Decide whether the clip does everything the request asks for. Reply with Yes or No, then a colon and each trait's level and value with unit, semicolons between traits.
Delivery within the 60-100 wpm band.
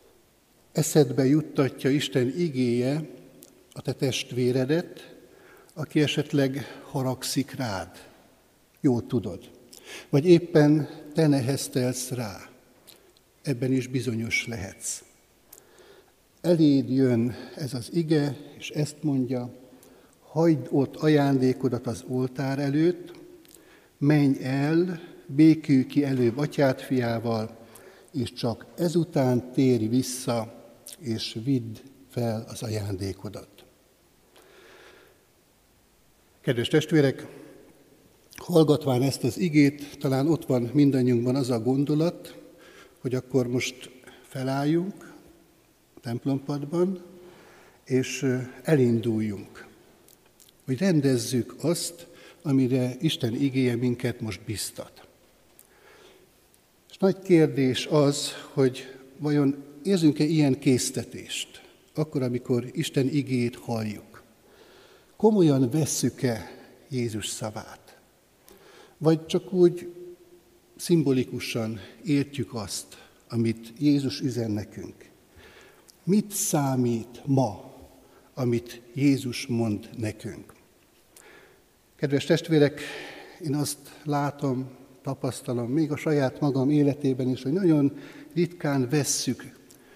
Yes: slow, 90 wpm